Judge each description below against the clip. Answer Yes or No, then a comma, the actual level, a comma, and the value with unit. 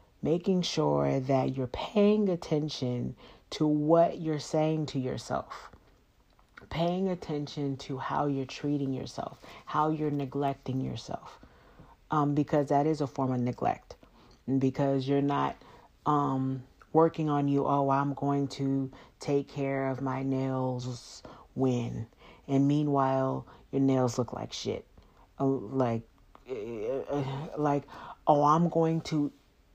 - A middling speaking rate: No, slow, 125 wpm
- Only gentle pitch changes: Yes, narrow, 2.2 semitones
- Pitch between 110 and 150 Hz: Yes, medium, 140 Hz